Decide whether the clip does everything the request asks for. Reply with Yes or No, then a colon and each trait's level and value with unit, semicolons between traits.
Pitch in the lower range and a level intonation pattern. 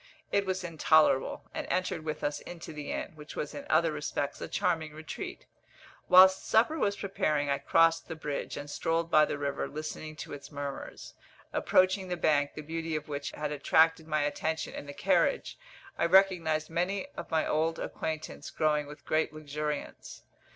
No: medium, 155 Hz; narrow, 2.1 semitones